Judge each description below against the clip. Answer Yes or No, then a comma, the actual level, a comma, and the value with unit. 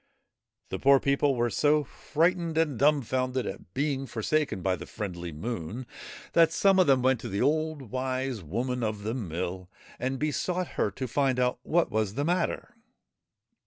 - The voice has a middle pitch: No, low, 130 Hz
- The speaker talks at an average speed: Yes, average, 165 wpm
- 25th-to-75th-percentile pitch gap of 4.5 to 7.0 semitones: Yes, average, 5.3 semitones